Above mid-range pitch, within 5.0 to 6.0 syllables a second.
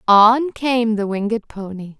No: high, 220 Hz; 3.9 syllables/s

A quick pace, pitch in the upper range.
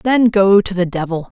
Yes: fast, 215 wpm; high, 195 Hz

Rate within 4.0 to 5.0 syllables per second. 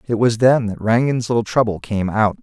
No: 5.3 syllables/s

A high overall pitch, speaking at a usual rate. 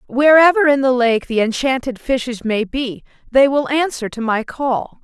Yes: very high, 255 Hz; average, 180 wpm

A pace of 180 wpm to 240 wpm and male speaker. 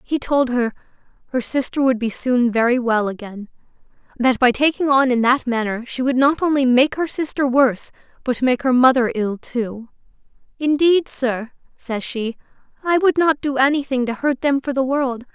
No: average, 185 wpm; female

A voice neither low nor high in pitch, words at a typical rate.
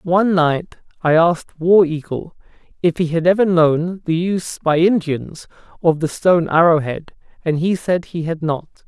Yes: medium, 165 Hz; average, 175 wpm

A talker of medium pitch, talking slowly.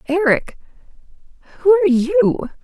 No: very high, 335 Hz; slow, 70 wpm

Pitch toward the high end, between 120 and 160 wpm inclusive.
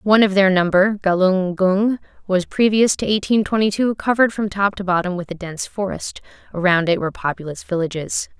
No: high, 195 Hz; average, 185 wpm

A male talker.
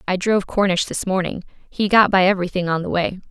No: female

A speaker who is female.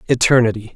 No: male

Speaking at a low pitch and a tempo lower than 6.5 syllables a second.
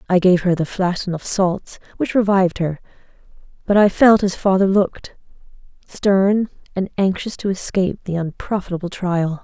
No: medium, 185 Hz; 5.0 syllables/s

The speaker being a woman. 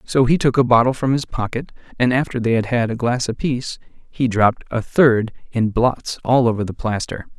No: male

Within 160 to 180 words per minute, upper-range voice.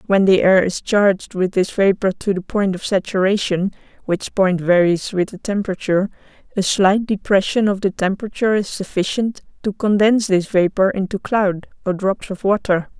Yes: average, 170 wpm; high, 195 Hz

